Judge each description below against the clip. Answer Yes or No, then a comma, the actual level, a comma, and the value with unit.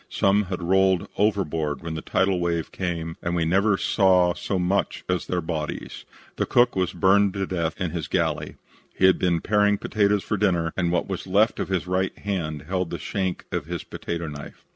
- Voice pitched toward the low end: Yes, very low, 90 Hz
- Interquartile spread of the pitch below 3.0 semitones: Yes, narrow, 2.6 semitones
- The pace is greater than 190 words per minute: Yes, average, 200 wpm